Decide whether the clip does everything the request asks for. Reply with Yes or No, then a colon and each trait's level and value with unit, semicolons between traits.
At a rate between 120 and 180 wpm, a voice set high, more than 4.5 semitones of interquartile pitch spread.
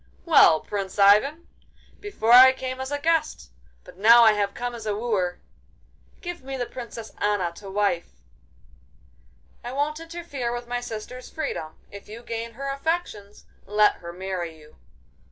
Yes: average, 155 wpm; high, 230 Hz; average, 4.9 semitones